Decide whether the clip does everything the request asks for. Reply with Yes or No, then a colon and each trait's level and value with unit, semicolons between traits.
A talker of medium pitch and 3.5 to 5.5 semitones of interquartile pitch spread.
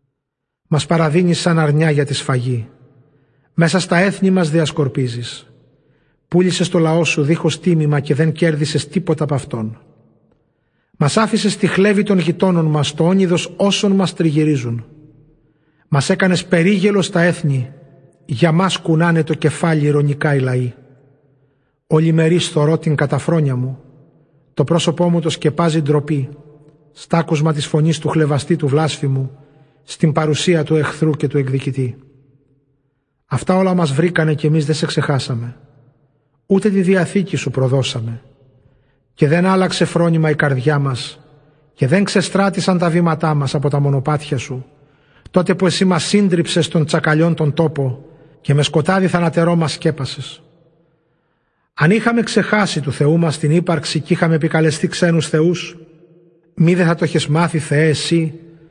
No: medium, 155 Hz; average, 2.9 semitones